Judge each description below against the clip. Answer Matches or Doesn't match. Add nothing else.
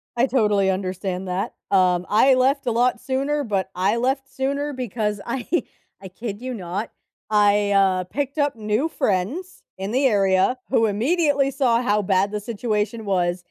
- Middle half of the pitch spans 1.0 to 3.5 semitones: Doesn't match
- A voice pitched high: Matches